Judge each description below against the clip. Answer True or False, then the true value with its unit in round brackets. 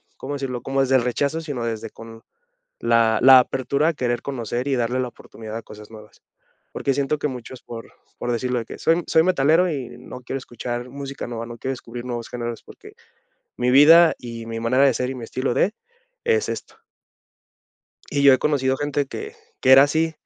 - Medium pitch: False (130 Hz)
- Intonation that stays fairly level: False (3.1 semitones)